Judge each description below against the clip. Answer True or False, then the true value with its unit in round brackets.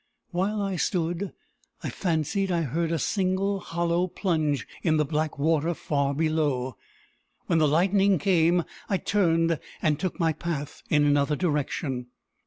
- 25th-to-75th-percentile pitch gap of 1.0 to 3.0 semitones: False (3.5 semitones)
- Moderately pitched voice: True (165 Hz)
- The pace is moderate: True (145 wpm)